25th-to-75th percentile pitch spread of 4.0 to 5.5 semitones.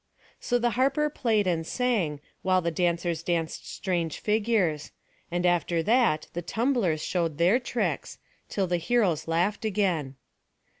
Yes: average, 5.1 semitones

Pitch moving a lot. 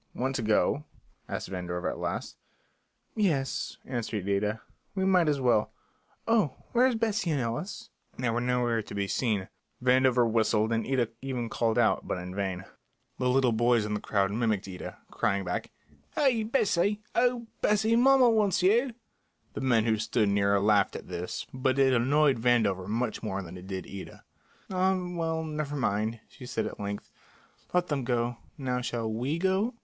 Yes: wide, 7.8 semitones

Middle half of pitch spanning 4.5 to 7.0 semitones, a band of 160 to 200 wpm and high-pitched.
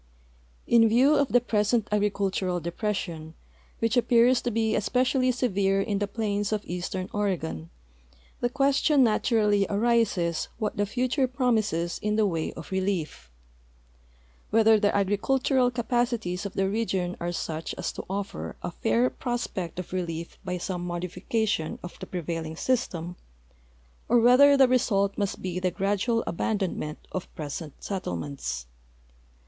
No: average, 4.9 semitones; average, 140 wpm; high, 200 Hz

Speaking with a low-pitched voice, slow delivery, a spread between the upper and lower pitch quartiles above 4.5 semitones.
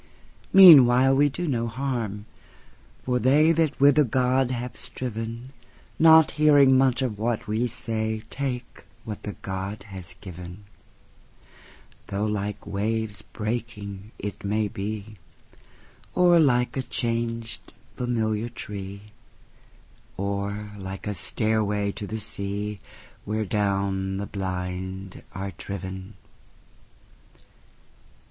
No: low, 110 Hz; slow, 95 wpm; average, 3.8 semitones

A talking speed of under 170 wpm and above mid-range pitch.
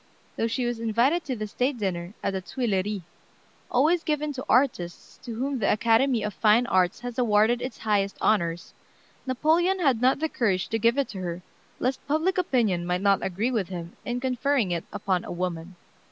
No: average, 190 wpm; high, 230 Hz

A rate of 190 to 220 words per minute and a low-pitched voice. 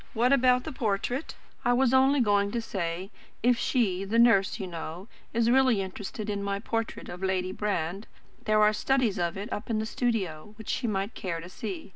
No: average, 200 wpm; high, 210 Hz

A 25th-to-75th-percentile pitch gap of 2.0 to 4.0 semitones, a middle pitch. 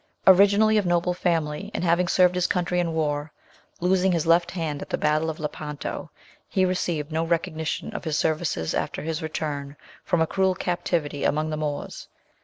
Yes: average, 2.8 semitones; medium, 165 Hz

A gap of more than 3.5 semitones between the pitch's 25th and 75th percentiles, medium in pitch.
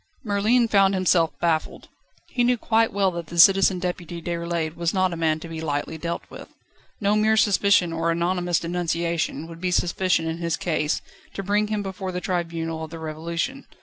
No: average, 3.0 semitones; medium, 175 Hz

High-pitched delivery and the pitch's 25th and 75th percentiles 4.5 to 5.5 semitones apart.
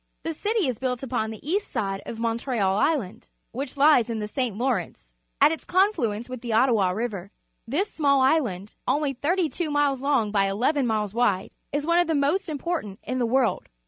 Yes: very high, 255 Hz; average, 5.2 semitones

